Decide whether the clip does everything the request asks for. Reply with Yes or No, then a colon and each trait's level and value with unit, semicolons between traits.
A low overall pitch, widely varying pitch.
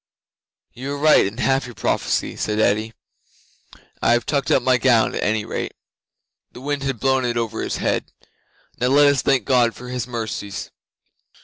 No: low, 125 Hz; average, 3.1 semitones